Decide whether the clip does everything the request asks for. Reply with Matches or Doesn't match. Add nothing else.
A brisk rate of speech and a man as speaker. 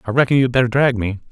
Matches